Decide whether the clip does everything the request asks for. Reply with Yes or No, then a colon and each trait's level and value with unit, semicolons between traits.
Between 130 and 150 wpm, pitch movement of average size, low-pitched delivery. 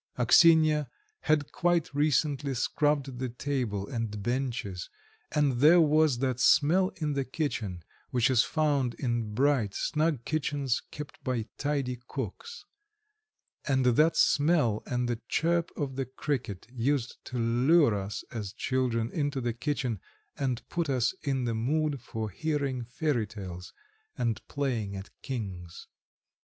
Yes: slow, 135 wpm; average, 4.2 semitones; low, 130 Hz